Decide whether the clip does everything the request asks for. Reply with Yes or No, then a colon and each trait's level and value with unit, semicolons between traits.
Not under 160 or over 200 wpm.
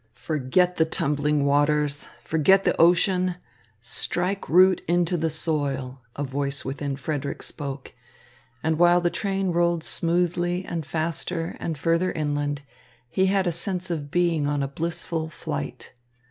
No: average, 140 wpm